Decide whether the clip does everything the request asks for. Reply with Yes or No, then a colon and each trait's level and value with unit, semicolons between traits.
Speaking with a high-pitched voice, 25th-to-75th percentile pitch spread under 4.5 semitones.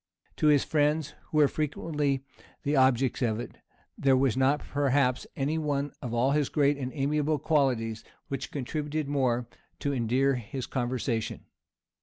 No: medium, 140 Hz; narrow, 2.5 semitones